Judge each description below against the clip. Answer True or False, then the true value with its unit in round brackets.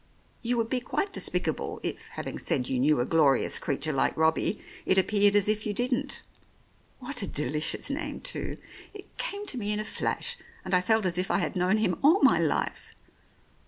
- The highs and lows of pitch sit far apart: True (7.4 semitones)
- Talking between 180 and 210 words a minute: True (195 wpm)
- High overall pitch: True (205 Hz)